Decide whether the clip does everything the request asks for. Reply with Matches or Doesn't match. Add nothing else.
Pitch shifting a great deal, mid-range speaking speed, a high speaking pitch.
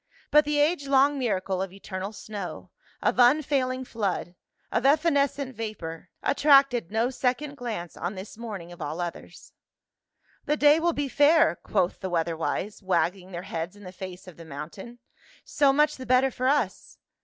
Matches